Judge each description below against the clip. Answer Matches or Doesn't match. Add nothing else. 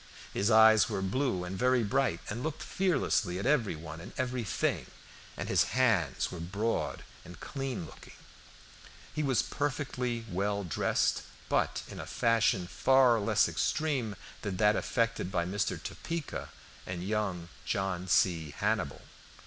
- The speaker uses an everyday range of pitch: Doesn't match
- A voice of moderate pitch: Doesn't match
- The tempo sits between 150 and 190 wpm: Doesn't match